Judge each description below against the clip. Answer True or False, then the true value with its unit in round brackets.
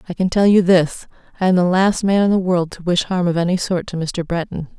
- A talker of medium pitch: True (180 Hz)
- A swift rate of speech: True (265 wpm)